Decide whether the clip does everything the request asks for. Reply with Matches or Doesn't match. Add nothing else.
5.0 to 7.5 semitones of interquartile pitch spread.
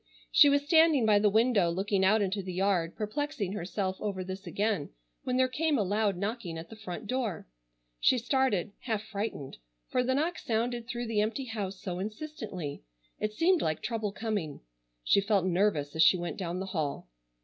Doesn't match